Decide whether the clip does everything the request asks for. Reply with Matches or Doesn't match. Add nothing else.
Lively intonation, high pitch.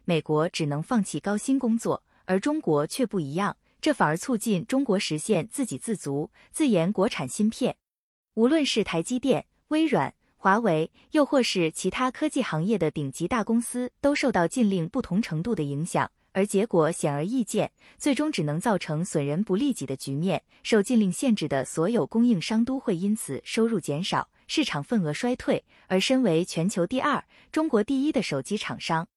Matches